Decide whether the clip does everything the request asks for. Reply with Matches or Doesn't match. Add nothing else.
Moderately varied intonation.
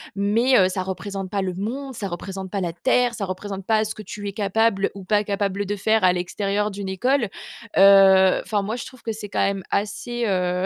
Doesn't match